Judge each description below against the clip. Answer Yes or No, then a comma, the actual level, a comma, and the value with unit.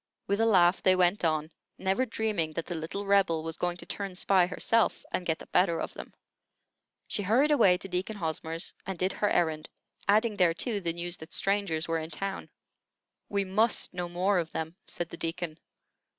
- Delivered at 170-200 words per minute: Yes, average, 195 wpm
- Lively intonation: No, average, 3.3 semitones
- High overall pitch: No, medium, 180 Hz